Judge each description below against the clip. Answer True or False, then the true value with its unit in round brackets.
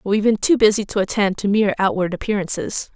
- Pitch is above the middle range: True (205 Hz)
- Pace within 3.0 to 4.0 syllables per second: False (6.5 syllables/s)